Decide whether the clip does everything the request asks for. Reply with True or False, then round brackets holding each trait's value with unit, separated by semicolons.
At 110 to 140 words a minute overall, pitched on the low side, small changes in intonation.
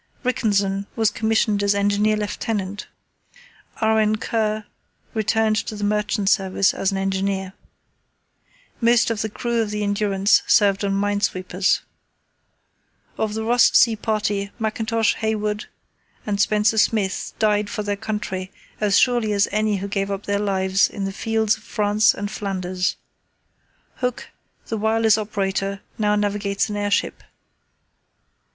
False (135 wpm; 210 Hz; 1.6 semitones)